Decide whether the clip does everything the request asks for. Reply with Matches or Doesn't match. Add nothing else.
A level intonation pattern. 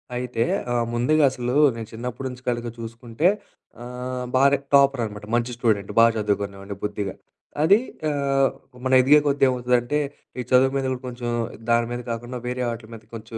Matches